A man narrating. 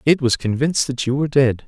Yes: male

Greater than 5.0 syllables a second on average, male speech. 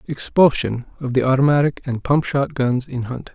Yes: 5.4 syllables/s; male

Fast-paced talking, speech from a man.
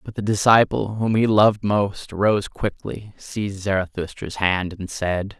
No: average, 155 wpm; male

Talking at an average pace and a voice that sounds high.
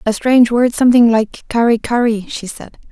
Yes: average, 185 wpm; high, 230 Hz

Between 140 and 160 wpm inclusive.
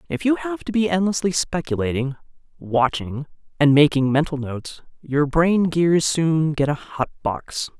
Yes: average, 155 wpm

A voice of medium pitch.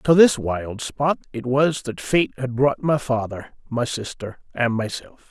No: low, 125 Hz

